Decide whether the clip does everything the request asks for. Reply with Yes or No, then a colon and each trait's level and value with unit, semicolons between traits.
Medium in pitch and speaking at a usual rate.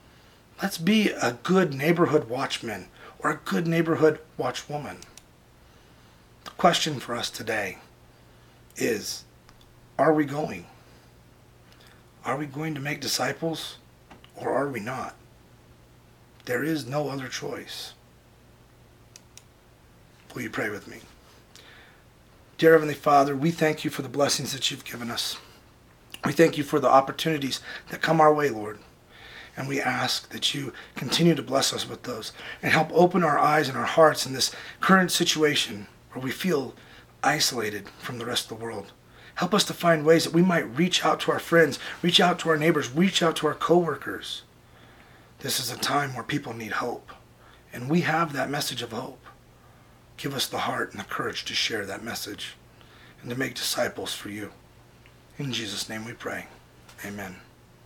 Yes: medium, 145 Hz; average, 165 wpm